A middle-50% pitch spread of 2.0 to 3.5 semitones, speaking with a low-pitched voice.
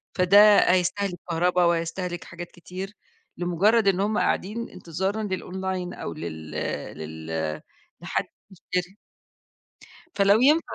No: average, 2.9 semitones; medium, 180 Hz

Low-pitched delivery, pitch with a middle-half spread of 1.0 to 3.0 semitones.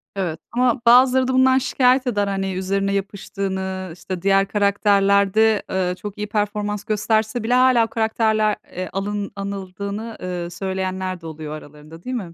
No: high, 200 Hz; average, 2.7 semitones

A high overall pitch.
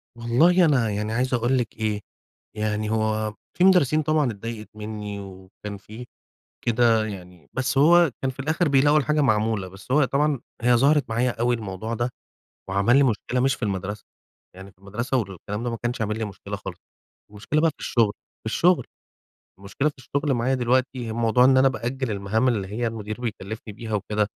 No: low, 115 Hz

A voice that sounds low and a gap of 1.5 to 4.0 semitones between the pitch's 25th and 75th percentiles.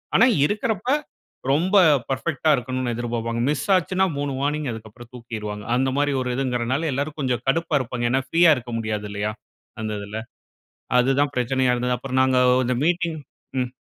Yes: low, 130 Hz; average, 3.7 semitones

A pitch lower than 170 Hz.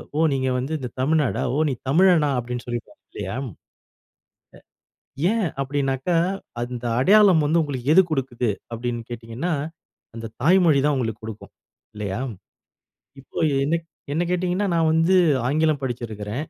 Yes: low, 135 Hz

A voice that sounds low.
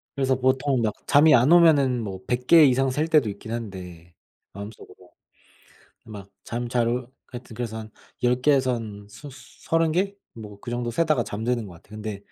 Yes: low, 120 Hz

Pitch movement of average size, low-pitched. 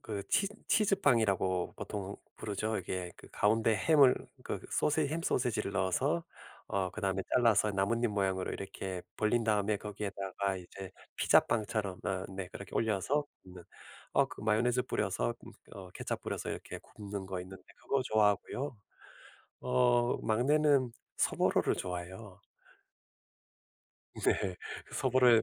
Yes: average, 4.1 semitones; low, 105 Hz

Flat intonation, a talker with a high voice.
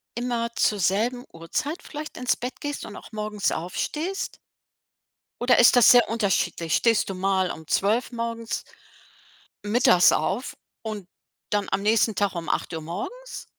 No: average, 4.2 semitones; high, 220 Hz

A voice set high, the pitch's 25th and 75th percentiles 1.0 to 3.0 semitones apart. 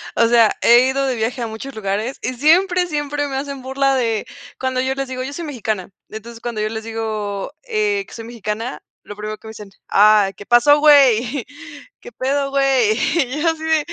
No: very high, 255 Hz; average, 4.2 semitones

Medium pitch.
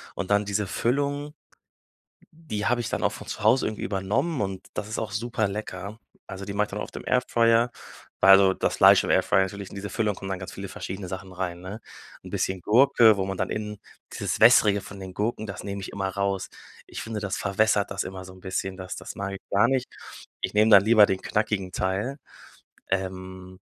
No: low, 100 Hz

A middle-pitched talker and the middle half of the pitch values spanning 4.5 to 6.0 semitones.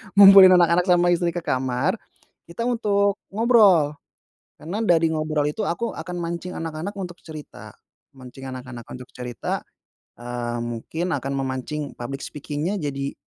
Yes: medium, 160 Hz; average, 5.3 semitones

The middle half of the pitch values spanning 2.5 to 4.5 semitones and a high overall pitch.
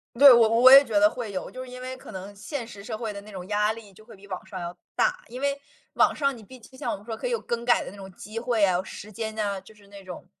Yes: average, 3.5 semitones; high, 220 Hz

